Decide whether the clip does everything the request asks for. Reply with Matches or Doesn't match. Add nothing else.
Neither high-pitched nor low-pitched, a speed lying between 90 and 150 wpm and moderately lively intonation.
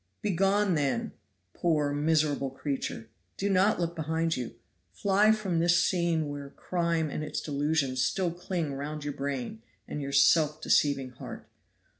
Matches